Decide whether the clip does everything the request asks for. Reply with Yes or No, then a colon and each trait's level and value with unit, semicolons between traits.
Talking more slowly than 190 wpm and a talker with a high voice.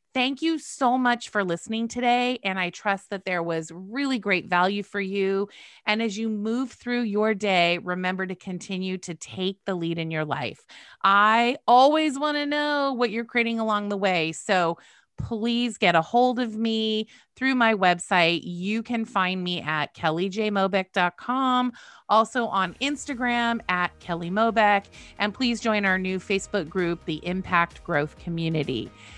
Yes: average, 160 wpm; high, 200 Hz